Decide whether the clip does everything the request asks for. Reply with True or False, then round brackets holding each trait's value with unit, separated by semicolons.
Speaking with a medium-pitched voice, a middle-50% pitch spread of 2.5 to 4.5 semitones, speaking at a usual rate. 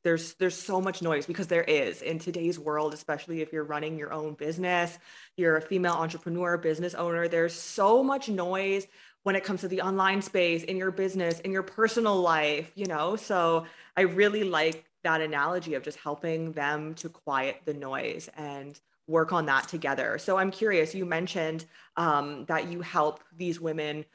True (170 Hz; 3.2 semitones; 185 wpm)